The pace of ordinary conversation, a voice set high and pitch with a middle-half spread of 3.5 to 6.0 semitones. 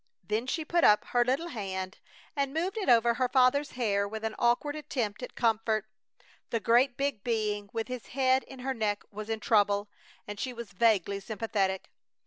Yes: average, 185 wpm; high, 230 Hz; average, 3.8 semitones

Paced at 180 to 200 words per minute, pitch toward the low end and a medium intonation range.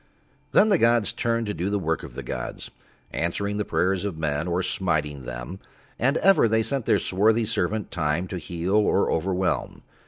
Yes: average, 185 wpm; very low, 95 Hz; average, 4.6 semitones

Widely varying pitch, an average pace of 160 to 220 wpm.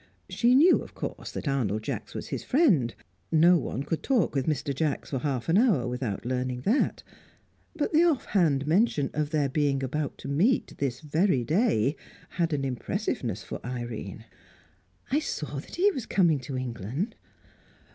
Yes: wide, 6.9 semitones; average, 170 wpm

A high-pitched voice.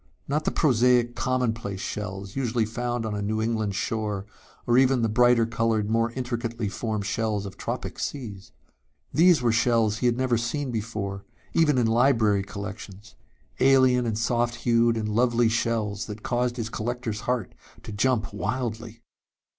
No: low, 115 Hz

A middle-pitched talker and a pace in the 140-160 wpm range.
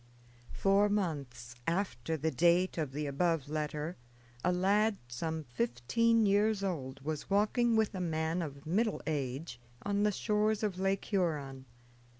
Yes: medium, 170 Hz; average, 145 wpm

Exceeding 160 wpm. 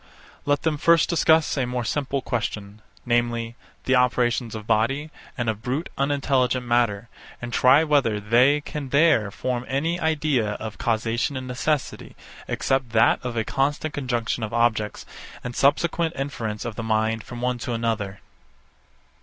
No: average, 155 wpm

